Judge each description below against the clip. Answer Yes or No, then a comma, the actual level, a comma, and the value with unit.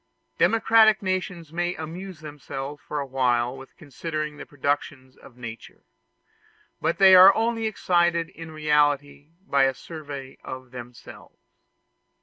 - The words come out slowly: Yes, slow, 130 wpm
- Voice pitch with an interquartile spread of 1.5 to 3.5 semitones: No, average, 4.6 semitones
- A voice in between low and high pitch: Yes, medium, 150 Hz